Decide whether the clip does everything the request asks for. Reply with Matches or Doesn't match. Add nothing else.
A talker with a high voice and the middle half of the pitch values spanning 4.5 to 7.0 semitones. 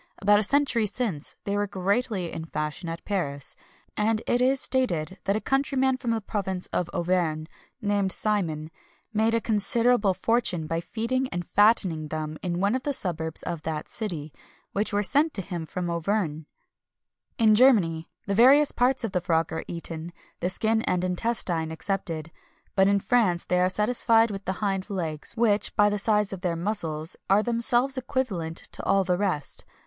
Matches